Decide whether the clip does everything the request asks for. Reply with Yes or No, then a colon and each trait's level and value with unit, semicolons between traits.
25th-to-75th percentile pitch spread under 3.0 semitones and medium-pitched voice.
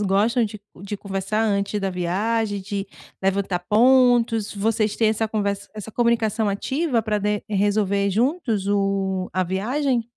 No: narrow, 2.4 semitones; high, 210 Hz